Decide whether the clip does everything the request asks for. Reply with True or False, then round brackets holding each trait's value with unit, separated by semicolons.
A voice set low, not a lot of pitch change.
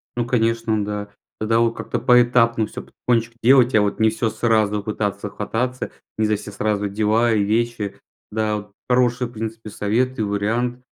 True (110 Hz; 2.3 semitones)